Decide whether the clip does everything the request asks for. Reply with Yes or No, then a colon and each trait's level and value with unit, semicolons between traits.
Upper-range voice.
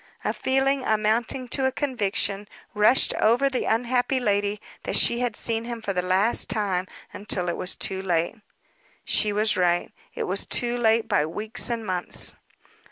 Yes: high, 215 Hz